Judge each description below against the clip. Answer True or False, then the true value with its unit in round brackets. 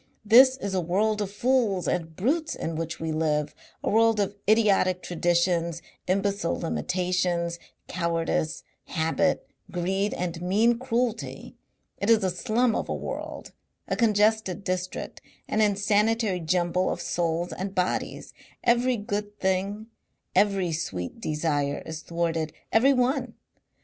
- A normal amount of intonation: True (4.1 semitones)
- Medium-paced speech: False (130 wpm)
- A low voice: False (190 Hz)